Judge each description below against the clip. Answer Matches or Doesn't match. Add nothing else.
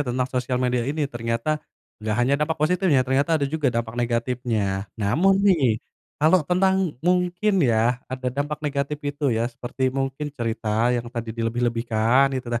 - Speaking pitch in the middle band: Doesn't match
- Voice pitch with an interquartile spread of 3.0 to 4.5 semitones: Matches